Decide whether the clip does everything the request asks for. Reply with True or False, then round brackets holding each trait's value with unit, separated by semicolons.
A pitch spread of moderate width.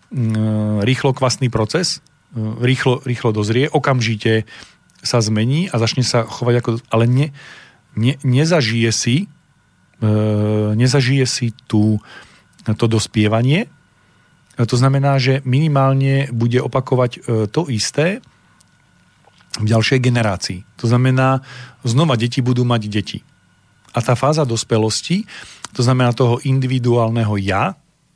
True (3.4 semitones)